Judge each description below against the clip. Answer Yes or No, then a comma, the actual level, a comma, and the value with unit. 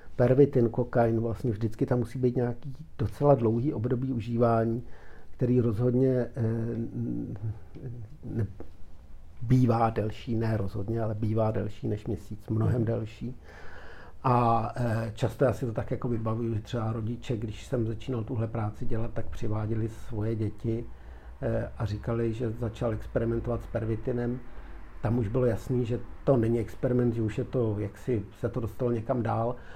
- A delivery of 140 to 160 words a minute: Yes, average, 155 wpm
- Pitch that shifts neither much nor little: No, narrow, 1.9 semitones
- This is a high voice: No, low, 115 Hz